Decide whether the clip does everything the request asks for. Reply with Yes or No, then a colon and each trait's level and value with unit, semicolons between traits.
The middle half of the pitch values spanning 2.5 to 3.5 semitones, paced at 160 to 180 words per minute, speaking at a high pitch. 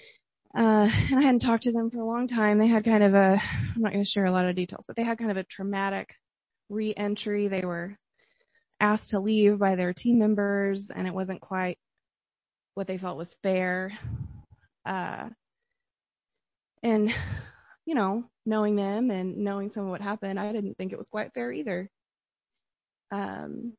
Yes: average, 2.9 semitones; average, 175 wpm; high, 205 Hz